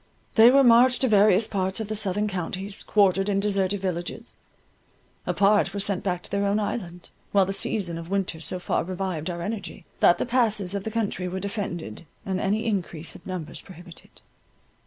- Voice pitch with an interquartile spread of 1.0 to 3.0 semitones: Yes, narrow, 2.5 semitones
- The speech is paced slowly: No, average, 185 wpm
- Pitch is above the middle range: Yes, high, 195 Hz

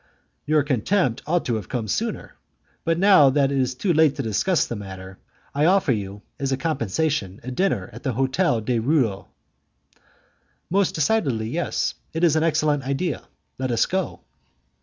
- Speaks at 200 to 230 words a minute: No, average, 165 wpm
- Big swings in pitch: Yes, wide, 5.9 semitones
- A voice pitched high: No, medium, 140 Hz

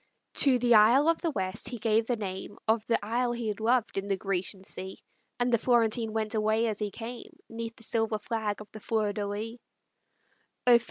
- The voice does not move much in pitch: Yes, narrow, 2.2 semitones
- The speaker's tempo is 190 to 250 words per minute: Yes, fast, 205 wpm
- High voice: Yes, high, 220 Hz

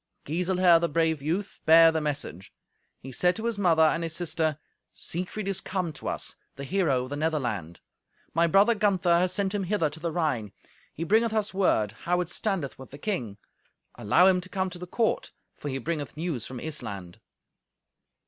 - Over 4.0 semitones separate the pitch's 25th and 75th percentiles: Yes, average, 4.4 semitones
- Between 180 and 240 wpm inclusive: Yes, average, 190 wpm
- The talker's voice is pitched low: No, medium, 165 Hz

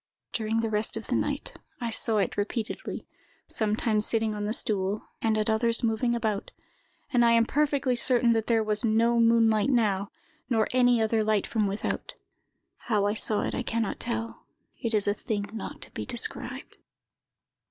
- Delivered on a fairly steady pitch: Yes, narrow, 1.6 semitones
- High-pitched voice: Yes, high, 225 Hz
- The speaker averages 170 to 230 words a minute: Yes, average, 180 wpm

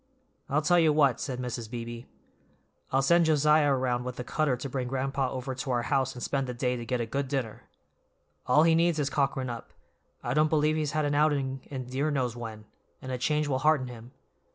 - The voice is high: No, low, 135 Hz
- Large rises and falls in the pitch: No, average, 3.2 semitones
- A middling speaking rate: No, fast, 220 wpm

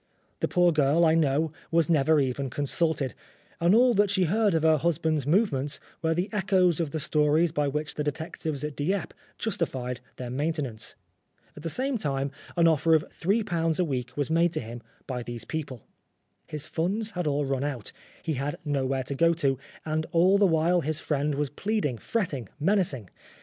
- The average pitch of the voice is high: No, medium, 155 Hz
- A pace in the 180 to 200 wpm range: Yes, average, 190 wpm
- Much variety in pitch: No, average, 3.6 semitones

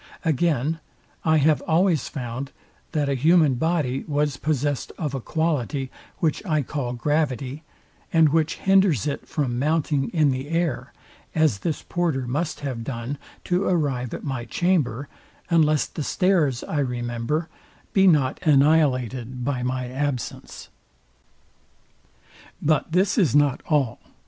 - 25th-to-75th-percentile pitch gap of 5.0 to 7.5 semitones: No, average, 3.8 semitones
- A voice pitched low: No, medium, 145 Hz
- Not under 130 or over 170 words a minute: Yes, slow, 135 wpm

